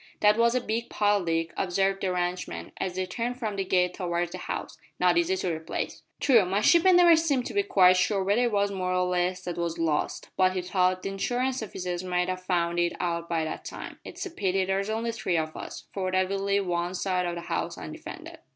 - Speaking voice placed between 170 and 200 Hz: Yes, medium, 185 Hz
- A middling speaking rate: No, fast, 235 wpm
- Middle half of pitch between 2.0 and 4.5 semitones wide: Yes, average, 2.9 semitones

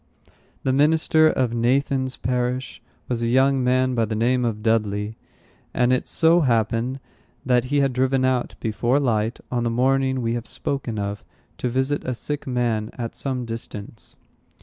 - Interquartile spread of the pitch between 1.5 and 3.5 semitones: Yes, narrow, 2.4 semitones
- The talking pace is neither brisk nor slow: Yes, average, 165 wpm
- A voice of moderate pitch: No, low, 125 Hz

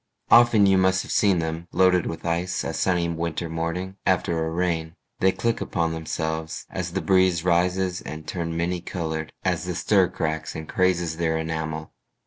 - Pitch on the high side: No, very low, 85 Hz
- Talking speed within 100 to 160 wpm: No, average, 175 wpm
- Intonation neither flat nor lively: No, narrow, 2.3 semitones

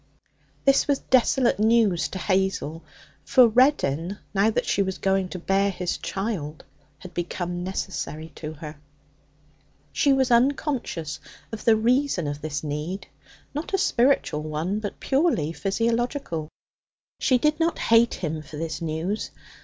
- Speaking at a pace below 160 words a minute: Yes, average, 140 wpm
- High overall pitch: Yes, high, 195 Hz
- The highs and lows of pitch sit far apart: Yes, wide, 6.9 semitones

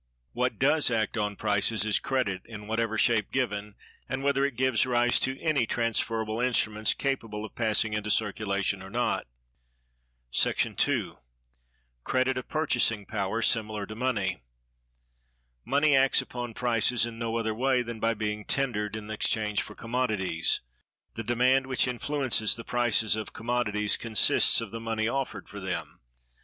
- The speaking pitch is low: Yes, low, 115 Hz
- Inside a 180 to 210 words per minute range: No, average, 150 wpm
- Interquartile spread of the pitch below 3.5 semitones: Yes, average, 2.9 semitones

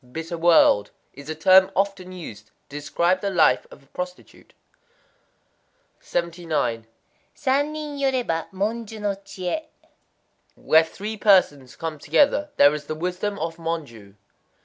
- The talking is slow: Yes, slow, 125 wpm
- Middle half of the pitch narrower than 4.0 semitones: No, average, 4.7 semitones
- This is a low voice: No, medium, 175 Hz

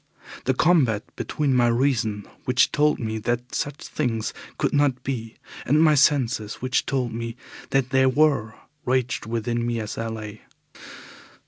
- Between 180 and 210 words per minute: No, average, 150 wpm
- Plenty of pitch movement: No, average, 3.3 semitones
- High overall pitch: No, low, 125 Hz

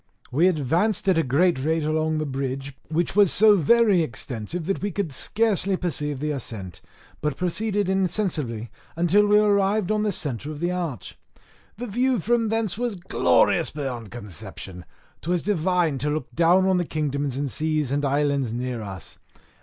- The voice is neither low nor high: Yes, medium, 160 Hz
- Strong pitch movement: Yes, wide, 6.0 semitones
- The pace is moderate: Yes, average, 170 wpm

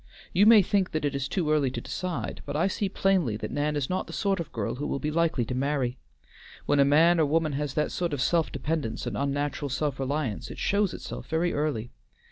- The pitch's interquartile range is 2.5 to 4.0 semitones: Yes, average, 3.6 semitones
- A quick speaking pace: Yes, fast, 235 wpm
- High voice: No, medium, 150 Hz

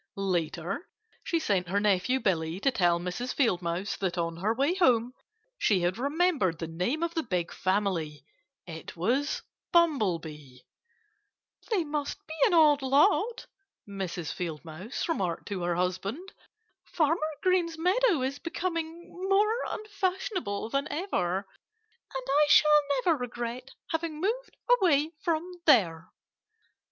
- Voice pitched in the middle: No, very high, 250 Hz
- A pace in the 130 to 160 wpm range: Yes, slow, 135 wpm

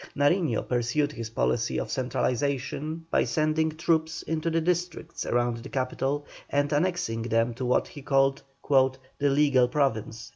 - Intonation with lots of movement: No, average, 4.1 semitones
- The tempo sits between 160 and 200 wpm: No, average, 145 wpm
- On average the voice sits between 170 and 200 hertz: No, medium, 140 Hz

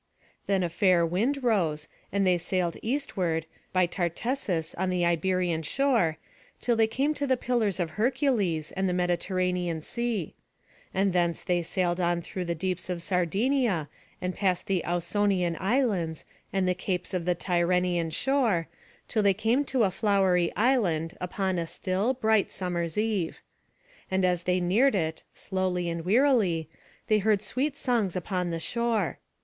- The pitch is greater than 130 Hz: Yes, medium, 185 Hz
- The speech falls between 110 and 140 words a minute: No, average, 155 wpm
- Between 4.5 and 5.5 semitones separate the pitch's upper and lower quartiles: No, average, 4.0 semitones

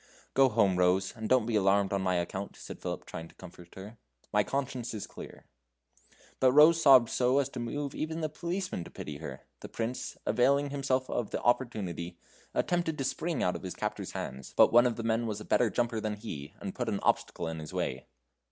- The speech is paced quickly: Yes, fast, 215 wpm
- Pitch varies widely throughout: Yes, wide, 5.7 semitones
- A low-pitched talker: Yes, low, 115 Hz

